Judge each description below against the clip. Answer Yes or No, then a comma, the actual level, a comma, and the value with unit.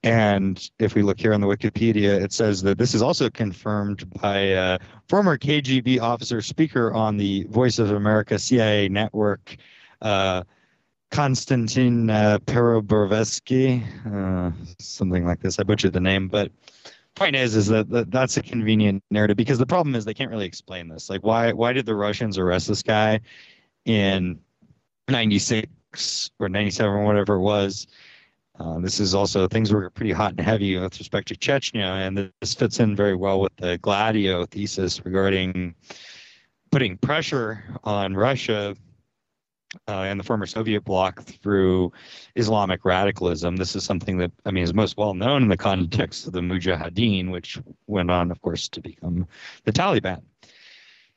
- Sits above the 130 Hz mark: No, low, 105 Hz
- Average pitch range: Yes, average, 3.1 semitones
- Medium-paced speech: Yes, average, 165 wpm